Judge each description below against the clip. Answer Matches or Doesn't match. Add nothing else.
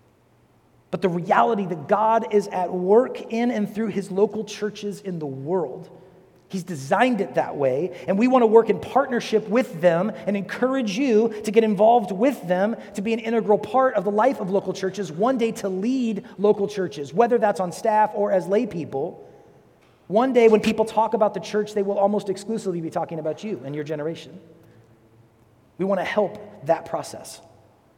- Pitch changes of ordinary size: Matches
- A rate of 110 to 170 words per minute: Doesn't match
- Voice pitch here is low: Doesn't match